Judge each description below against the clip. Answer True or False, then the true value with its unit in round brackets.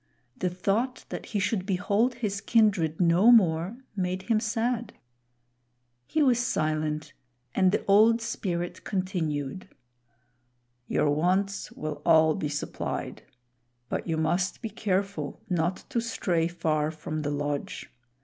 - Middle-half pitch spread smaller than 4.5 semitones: False (5.3 semitones)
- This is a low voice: False (185 Hz)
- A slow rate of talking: True (130 wpm)